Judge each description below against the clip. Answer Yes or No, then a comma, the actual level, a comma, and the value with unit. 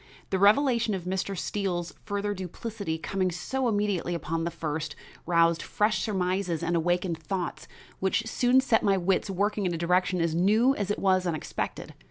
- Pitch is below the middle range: No, high, 190 Hz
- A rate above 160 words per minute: Yes, average, 170 wpm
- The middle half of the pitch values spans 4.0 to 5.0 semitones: No, average, 3.2 semitones